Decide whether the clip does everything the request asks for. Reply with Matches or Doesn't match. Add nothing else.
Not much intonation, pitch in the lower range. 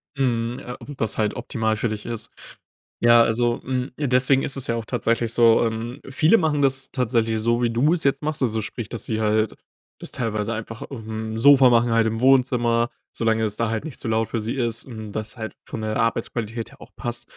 Matches